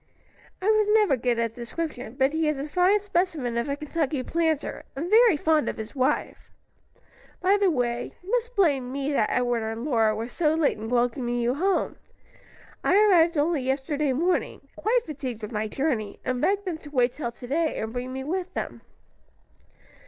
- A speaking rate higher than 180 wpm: Yes, average, 190 wpm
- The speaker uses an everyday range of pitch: No, wide, 5.9 semitones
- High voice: Yes, very high, 285 Hz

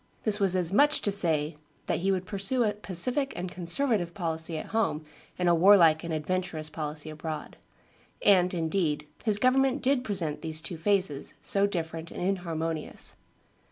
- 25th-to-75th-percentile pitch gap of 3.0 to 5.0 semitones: Yes, average, 4.0 semitones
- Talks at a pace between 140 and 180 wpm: Yes, average, 165 wpm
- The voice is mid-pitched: Yes, medium, 180 Hz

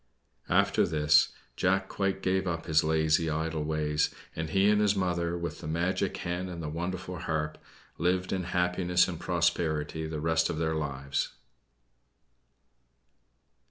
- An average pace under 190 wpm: Yes, average, 145 wpm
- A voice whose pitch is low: Yes, very low, 85 Hz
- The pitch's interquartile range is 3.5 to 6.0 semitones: No, average, 2.7 semitones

